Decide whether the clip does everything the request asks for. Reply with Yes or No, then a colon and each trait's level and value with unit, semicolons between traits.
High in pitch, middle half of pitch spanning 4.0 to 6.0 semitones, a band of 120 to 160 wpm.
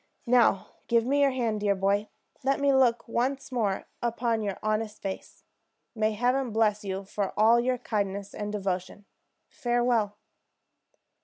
No: high, 220 Hz; average, 3.1 semitones; average, 150 wpm